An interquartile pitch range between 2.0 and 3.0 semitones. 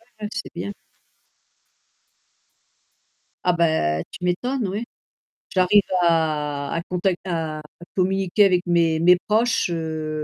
No: average, 3.4 semitones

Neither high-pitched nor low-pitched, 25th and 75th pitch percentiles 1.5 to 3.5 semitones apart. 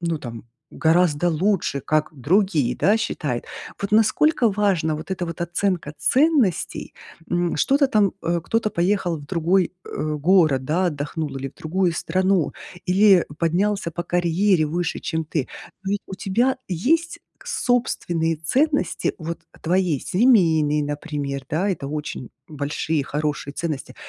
No: medium, 170 Hz; average, 4.2 semitones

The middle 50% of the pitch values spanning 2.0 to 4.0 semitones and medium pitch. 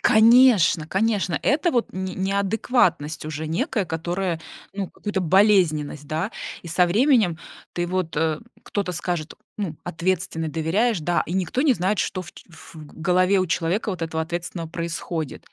Yes: average, 3.7 semitones; medium, 180 Hz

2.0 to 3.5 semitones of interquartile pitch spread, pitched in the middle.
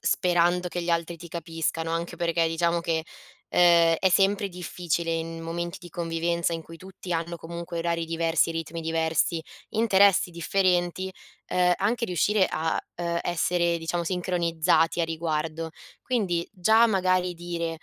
No: narrow, 1.4 semitones; medium, 170 Hz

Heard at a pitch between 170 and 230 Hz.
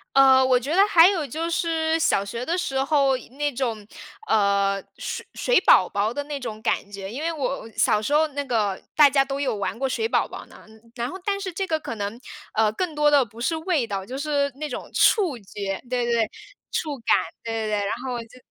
No: very high, 270 Hz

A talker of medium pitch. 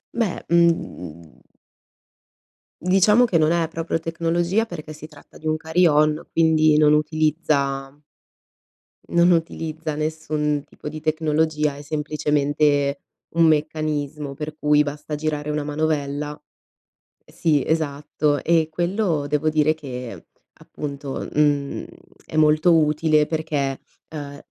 Yes: medium, 155 Hz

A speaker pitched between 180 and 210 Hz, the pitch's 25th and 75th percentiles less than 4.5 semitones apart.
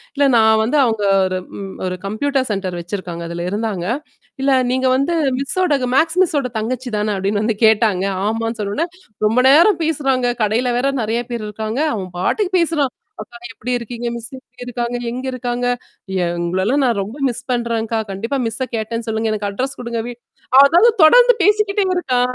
No: high, 235 Hz; average, 4.1 semitones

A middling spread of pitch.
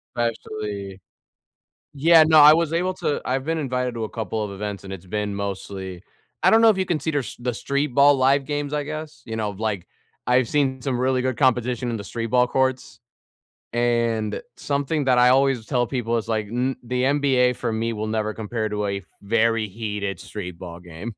Yes: average, 4.2 semitones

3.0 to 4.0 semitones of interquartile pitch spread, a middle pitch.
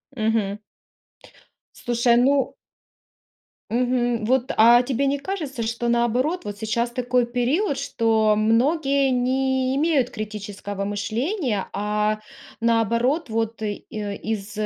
No: average, 3.4 semitones; high, 235 Hz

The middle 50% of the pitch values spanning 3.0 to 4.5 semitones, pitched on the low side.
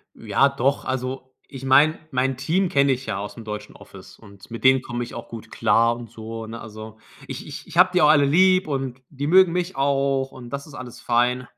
Yes: average, 3.3 semitones; low, 130 Hz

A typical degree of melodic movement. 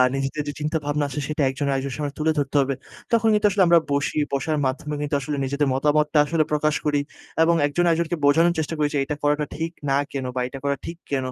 No: narrow, 2.1 semitones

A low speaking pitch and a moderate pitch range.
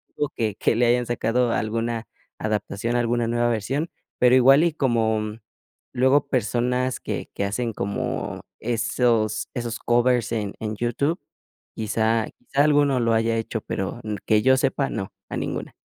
No: low, 120 Hz; narrow, 2.2 semitones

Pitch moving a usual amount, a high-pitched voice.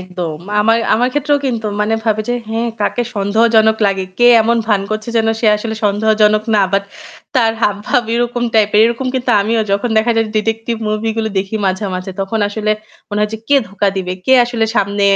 No: narrow, 2.2 semitones; high, 220 Hz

